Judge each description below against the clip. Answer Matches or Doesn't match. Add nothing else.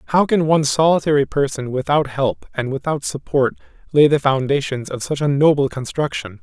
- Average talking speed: Matches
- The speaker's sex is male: Matches